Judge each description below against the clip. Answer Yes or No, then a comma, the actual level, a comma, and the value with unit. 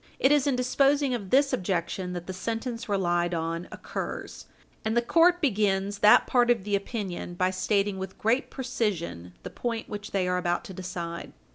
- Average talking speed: Yes, average, 185 wpm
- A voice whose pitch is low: No, high, 200 Hz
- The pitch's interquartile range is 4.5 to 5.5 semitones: Yes, average, 5.0 semitones